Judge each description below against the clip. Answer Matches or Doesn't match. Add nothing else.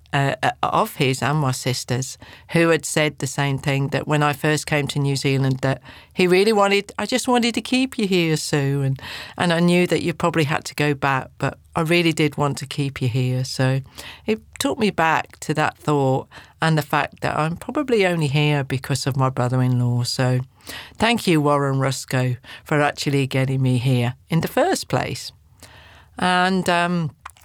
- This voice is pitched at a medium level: Matches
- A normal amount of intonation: Matches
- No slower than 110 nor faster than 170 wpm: Doesn't match